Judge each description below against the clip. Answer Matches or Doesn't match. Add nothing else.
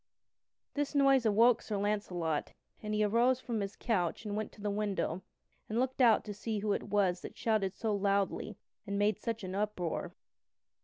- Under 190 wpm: Matches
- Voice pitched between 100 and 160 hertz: Doesn't match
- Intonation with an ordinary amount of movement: Doesn't match